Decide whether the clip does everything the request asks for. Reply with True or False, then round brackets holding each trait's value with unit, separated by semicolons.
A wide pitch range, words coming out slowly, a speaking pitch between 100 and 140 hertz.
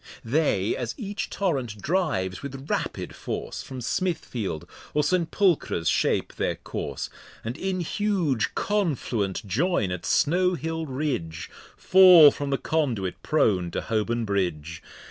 True (8.9 semitones; 125 wpm; 135 Hz)